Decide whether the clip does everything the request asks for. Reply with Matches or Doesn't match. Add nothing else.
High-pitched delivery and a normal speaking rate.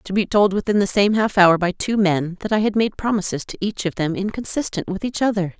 Doesn't match